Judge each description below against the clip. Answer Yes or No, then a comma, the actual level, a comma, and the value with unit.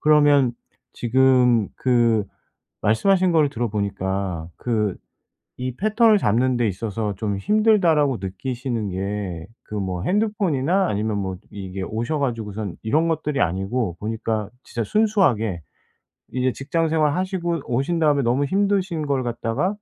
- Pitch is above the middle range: No, low, 125 Hz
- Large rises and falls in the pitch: Yes, wide, 7.2 semitones